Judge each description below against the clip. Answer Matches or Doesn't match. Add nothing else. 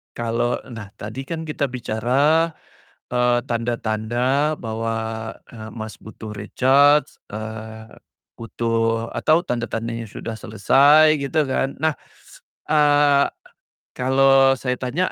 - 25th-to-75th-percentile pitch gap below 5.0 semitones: Matches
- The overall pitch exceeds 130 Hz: Doesn't match